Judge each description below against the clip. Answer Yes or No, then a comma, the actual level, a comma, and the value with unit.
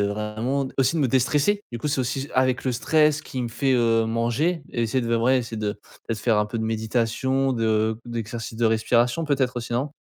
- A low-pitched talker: Yes, low, 120 Hz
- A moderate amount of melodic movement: Yes, average, 3.0 semitones